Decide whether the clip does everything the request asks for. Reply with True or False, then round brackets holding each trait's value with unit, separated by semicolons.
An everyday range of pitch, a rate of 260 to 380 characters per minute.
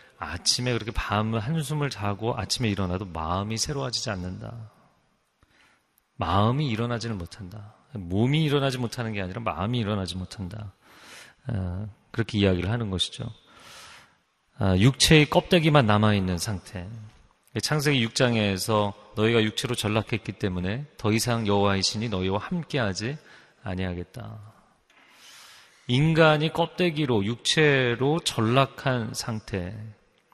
True (4.1 semitones; 285 characters per minute)